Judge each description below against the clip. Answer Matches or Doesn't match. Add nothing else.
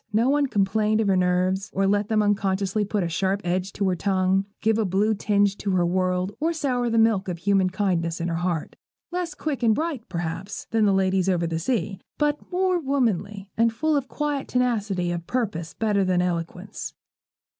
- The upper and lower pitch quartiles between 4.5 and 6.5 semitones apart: Doesn't match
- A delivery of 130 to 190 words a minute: Doesn't match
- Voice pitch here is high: Matches